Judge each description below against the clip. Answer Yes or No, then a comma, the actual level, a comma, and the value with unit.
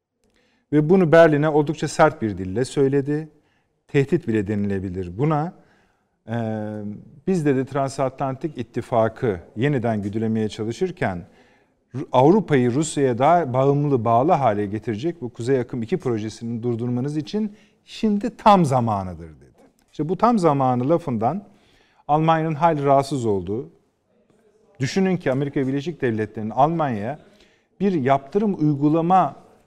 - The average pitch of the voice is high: No, medium, 140 Hz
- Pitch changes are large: Yes, wide, 6.4 semitones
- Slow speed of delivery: No, average, 110 wpm